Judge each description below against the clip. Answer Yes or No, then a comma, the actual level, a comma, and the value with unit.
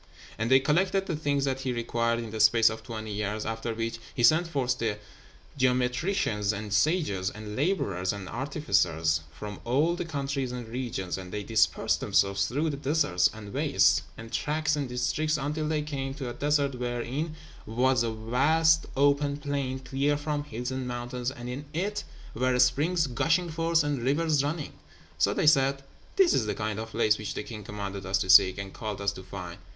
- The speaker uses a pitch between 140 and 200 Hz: No, low, 125 Hz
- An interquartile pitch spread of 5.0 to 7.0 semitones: Yes, average, 5.3 semitones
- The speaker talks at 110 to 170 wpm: No, average, 190 wpm